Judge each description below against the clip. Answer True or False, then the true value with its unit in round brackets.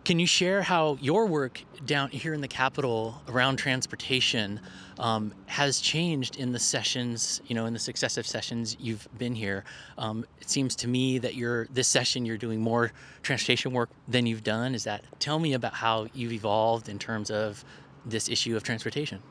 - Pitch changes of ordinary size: True (3.0 semitones)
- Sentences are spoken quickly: False (185 wpm)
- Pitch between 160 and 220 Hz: False (120 Hz)